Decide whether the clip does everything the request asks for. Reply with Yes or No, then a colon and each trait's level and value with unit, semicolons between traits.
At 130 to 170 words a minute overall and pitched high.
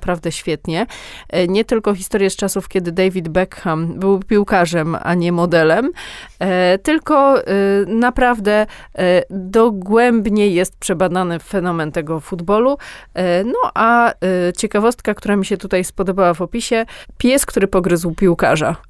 No: average, 115 wpm; high, 195 Hz